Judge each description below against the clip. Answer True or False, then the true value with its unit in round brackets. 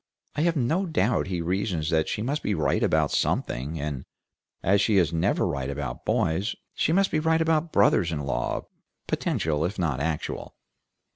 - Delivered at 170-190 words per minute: True (180 wpm)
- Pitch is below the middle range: True (90 Hz)